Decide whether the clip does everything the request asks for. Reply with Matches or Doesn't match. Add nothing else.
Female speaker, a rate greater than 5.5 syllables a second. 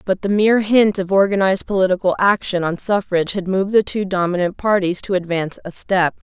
Matches